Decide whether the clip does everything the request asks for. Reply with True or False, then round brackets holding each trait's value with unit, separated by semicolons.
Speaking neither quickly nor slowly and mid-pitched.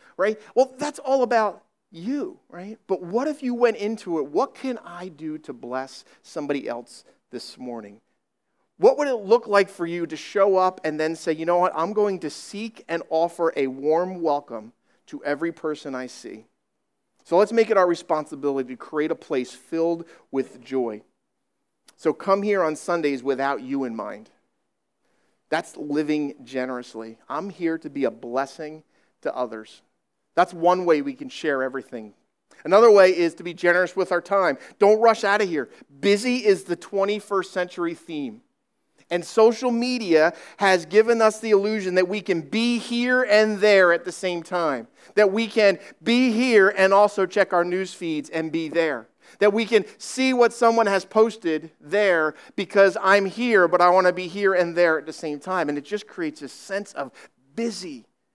True (185 wpm; 180 Hz)